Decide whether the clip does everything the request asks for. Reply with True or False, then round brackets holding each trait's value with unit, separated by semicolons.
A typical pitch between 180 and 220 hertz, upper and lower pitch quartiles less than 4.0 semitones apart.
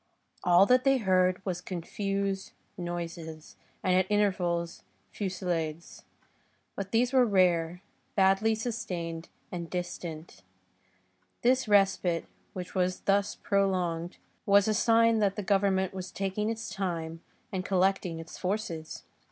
True (190 Hz; 2.7 semitones)